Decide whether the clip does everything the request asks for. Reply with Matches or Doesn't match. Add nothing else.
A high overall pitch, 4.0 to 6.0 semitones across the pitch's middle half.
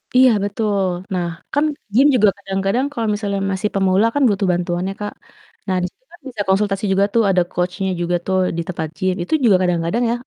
Doesn't match